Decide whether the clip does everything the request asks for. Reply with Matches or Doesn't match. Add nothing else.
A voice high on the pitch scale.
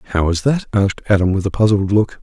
Doesn't match